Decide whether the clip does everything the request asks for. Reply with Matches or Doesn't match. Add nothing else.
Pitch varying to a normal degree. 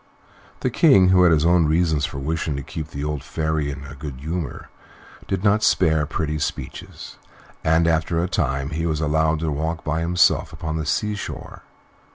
Doesn't match